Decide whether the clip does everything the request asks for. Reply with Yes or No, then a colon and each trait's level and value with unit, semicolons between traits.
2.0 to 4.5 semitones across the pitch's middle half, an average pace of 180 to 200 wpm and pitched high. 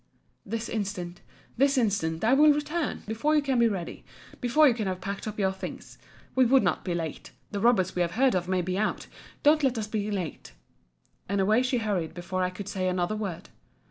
No: average, 5.0 semitones; average, 190 wpm; high, 205 Hz